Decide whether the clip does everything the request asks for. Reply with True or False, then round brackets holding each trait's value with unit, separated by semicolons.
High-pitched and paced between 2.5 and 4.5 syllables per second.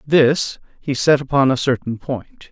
False (135 Hz; 4.1 syllables/s)